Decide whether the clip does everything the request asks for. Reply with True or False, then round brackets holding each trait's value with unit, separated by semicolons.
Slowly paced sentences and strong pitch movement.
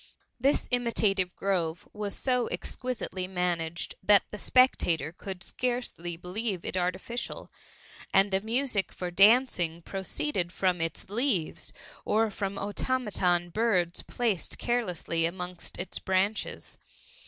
False (115 wpm; 4.5 semitones)